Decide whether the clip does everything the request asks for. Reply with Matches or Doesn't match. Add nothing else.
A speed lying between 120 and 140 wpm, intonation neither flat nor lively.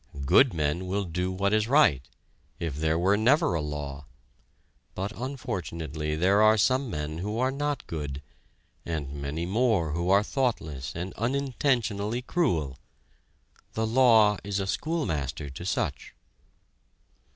Doesn't match